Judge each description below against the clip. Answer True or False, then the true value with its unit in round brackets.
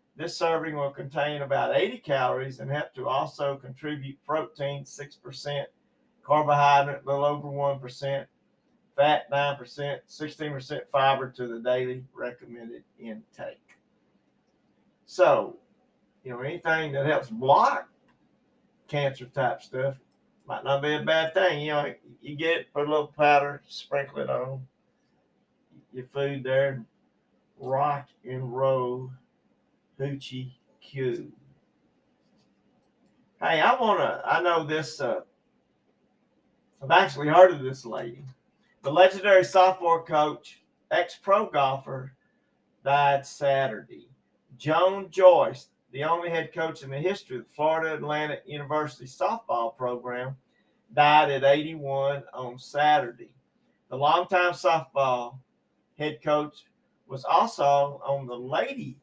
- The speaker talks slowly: True (120 wpm)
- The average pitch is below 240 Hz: True (140 Hz)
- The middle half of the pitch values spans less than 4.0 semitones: True (2.5 semitones)